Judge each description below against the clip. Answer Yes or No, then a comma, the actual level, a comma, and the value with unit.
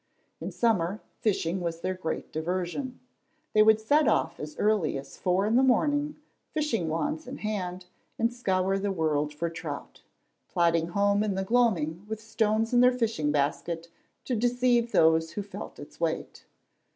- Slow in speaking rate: No, average, 165 wpm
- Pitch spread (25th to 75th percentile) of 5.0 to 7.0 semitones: Yes, wide, 5.6 semitones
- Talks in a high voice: Yes, high, 195 Hz